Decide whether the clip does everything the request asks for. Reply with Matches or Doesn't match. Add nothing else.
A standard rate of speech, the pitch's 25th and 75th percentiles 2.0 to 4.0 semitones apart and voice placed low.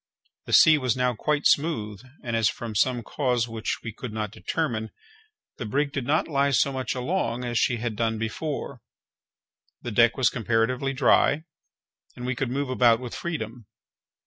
Matches